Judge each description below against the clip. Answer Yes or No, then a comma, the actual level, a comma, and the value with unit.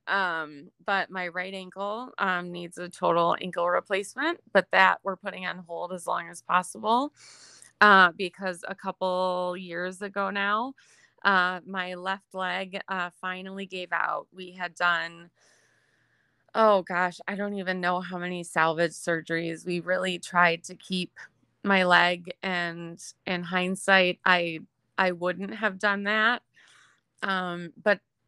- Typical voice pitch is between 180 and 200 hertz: Yes, medium, 185 Hz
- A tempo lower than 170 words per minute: Yes, average, 140 wpm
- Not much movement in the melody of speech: Yes, narrow, 1.8 semitones